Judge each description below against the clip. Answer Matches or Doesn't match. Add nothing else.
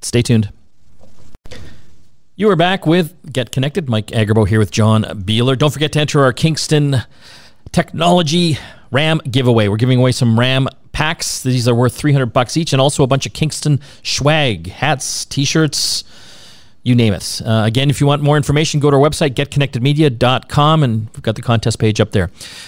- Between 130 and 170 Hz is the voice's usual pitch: Matches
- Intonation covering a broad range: Doesn't match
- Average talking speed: Matches